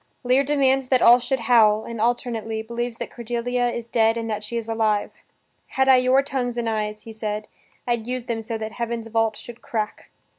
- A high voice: Yes, high, 235 Hz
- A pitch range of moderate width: No, narrow, 1.9 semitones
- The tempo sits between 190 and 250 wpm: Yes, average, 200 wpm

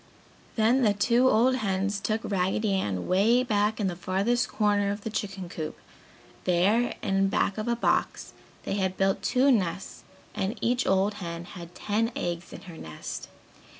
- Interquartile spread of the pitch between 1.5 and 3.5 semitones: Yes, average, 3.0 semitones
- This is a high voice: Yes, high, 200 Hz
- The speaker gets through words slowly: No, average, 170 wpm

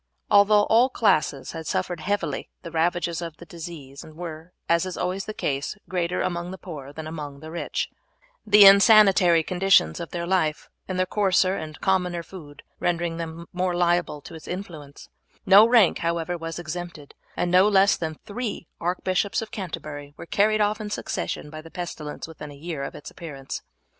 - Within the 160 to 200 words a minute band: Yes, average, 180 wpm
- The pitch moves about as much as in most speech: Yes, average, 3.2 semitones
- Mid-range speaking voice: Yes, medium, 175 Hz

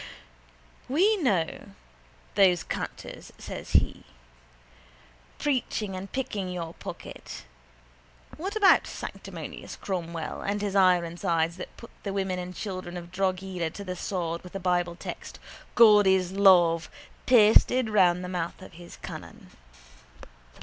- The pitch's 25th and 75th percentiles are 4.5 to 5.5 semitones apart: No, average, 2.8 semitones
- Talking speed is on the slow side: Yes, slow, 125 wpm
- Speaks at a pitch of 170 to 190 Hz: Yes, medium, 185 Hz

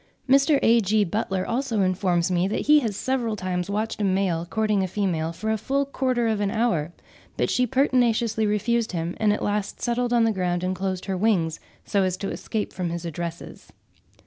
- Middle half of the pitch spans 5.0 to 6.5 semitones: No, average, 4.0 semitones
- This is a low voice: No, high, 205 Hz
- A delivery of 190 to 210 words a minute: Yes, average, 200 wpm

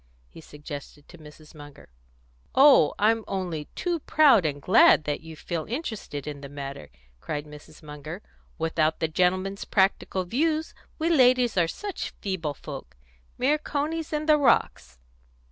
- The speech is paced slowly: No, average, 145 wpm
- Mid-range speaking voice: Yes, medium, 180 Hz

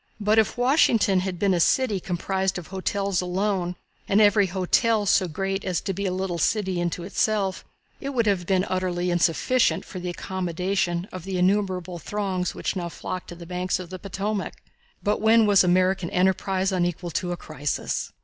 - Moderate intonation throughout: No, narrow, 2.0 semitones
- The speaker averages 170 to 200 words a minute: Yes, average, 180 wpm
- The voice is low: No, medium, 185 Hz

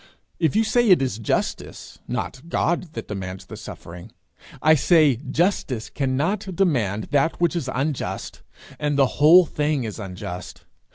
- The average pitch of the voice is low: No, medium, 145 Hz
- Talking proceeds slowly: No, average, 150 wpm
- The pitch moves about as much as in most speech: No, wide, 6.9 semitones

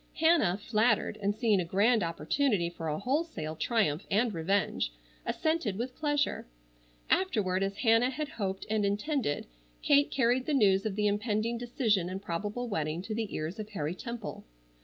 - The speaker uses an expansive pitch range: No, average, 4.5 semitones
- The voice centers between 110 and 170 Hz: No, high, 210 Hz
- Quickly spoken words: No, average, 160 wpm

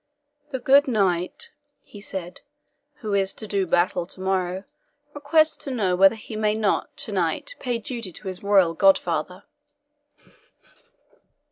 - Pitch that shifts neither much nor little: Yes, average, 4.1 semitones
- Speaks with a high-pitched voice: Yes, high, 200 Hz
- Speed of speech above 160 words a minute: No, slow, 135 wpm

